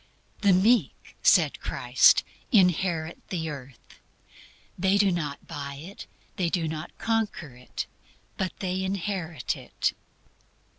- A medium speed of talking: No, slow, 115 wpm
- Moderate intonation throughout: Yes, average, 3.9 semitones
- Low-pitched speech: No, medium, 180 Hz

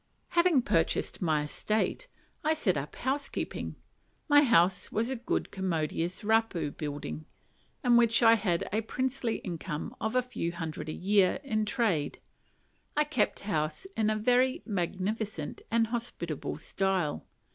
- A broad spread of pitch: Yes, wide, 6.0 semitones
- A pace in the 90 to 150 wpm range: Yes, average, 140 wpm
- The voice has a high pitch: Yes, high, 210 Hz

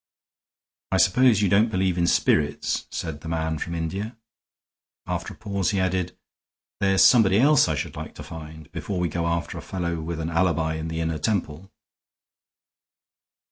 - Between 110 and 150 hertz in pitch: No, very low, 85 Hz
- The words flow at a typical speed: Yes, average, 170 wpm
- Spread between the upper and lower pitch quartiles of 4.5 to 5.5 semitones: No, average, 3.1 semitones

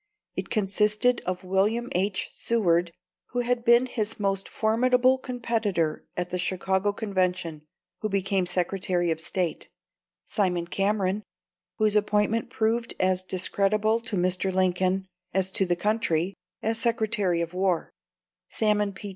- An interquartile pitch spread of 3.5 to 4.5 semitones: No, average, 3.1 semitones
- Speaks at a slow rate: Yes, slow, 130 wpm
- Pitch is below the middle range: No, high, 195 Hz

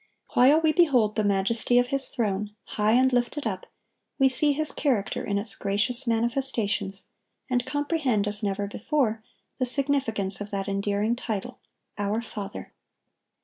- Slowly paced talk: No, average, 145 wpm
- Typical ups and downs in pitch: Yes, average, 4.3 semitones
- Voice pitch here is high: Yes, high, 225 Hz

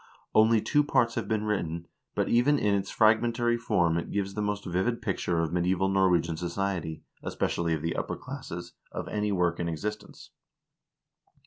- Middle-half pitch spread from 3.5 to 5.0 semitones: Yes, average, 4.1 semitones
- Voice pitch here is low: Yes, very low, 95 Hz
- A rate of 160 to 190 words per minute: Yes, average, 175 wpm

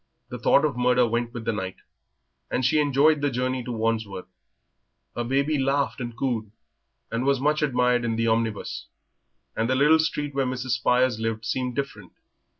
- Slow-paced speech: No, average, 175 wpm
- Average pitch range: Yes, average, 3.1 semitones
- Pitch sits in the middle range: No, low, 125 Hz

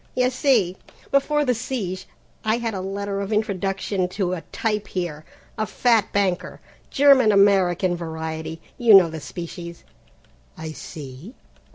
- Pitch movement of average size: Yes, average, 4.2 semitones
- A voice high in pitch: Yes, high, 195 Hz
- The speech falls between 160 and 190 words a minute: No, average, 140 wpm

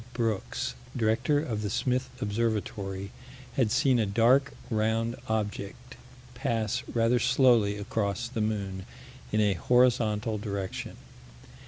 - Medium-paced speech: No, slow, 115 wpm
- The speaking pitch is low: Yes, low, 110 Hz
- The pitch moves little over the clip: No, average, 3.0 semitones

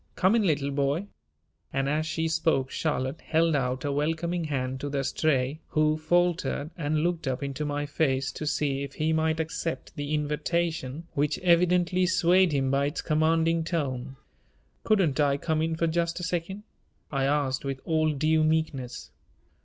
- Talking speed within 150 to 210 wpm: Yes, average, 170 wpm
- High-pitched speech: No, medium, 155 Hz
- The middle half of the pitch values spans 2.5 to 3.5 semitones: Yes, average, 2.9 semitones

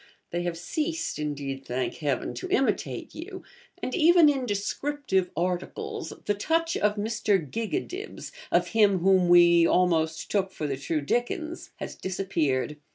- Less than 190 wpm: Yes, average, 145 wpm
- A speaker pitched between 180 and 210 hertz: Yes, high, 190 Hz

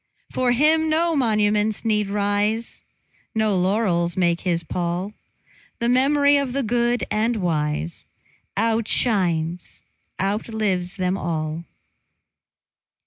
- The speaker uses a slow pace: Yes, slow, 100 wpm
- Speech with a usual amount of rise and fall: Yes, average, 5.0 semitones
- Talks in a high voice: Yes, high, 210 Hz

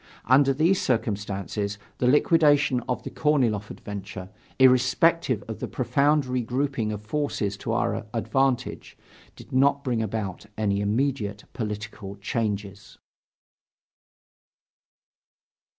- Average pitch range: Yes, average, 4.8 semitones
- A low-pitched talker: Yes, low, 115 Hz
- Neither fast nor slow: No, slow, 105 wpm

